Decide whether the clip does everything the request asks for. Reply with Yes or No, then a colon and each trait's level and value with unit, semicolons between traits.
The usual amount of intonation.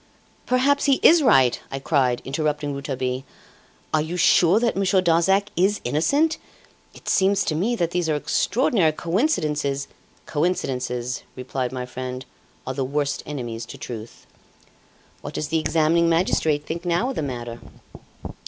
No: wide, 5.8 semitones